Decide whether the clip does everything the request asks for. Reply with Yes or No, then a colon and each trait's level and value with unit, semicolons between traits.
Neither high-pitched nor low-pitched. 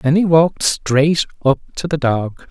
Yes: medium, 150 Hz